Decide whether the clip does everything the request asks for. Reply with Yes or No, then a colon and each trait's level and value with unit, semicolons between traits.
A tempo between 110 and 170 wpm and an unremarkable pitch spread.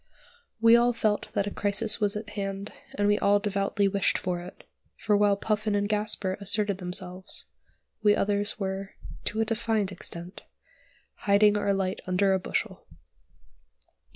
No: average, 150 wpm; narrow, 1.3 semitones